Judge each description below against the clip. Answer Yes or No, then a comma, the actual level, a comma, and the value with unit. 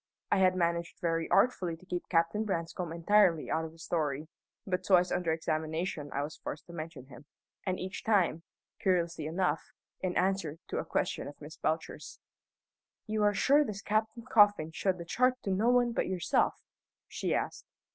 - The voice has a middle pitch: Yes, medium, 180 Hz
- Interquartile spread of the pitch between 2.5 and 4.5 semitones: Yes, average, 3.8 semitones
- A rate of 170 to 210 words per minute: Yes, average, 175 wpm